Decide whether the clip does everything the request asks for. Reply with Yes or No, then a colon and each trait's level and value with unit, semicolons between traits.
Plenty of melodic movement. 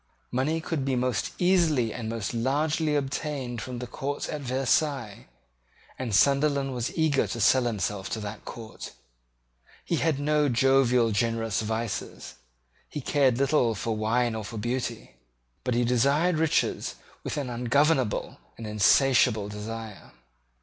No: average, 4.0 semitones